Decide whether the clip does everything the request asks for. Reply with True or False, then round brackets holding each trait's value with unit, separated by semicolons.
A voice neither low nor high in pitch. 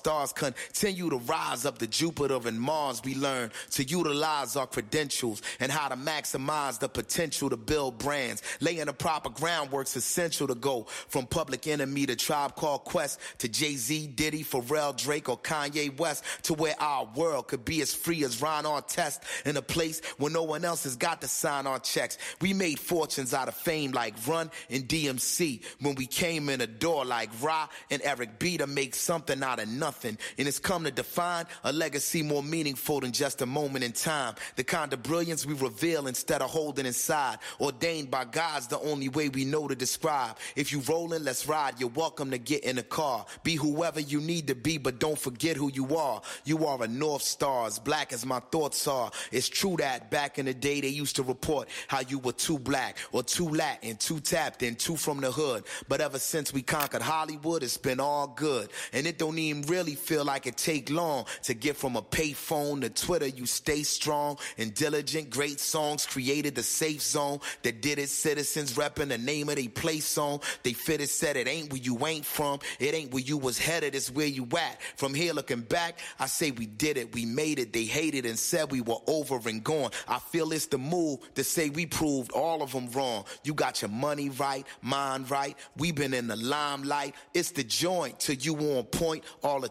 True (145 Hz)